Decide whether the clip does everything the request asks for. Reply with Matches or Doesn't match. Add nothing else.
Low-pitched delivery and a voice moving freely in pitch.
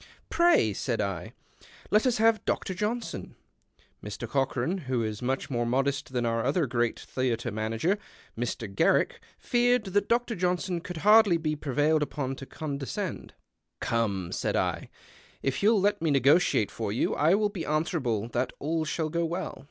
Doesn't match